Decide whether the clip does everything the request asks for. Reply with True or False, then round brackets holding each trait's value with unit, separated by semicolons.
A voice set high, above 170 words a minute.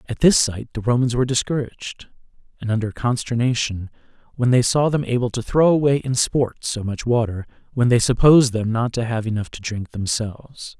False (120 Hz; 190 wpm)